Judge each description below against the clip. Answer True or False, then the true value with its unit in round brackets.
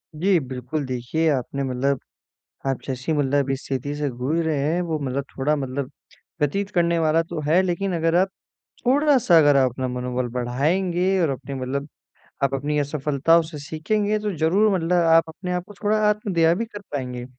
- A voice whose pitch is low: False (150 Hz)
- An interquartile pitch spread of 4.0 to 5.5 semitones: True (4.5 semitones)